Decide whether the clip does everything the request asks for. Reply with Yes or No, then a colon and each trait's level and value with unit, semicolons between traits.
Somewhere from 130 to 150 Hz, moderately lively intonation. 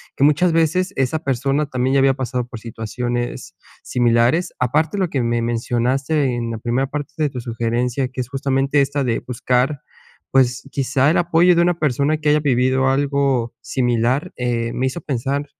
Yes: low, 135 Hz; average, 3.1 semitones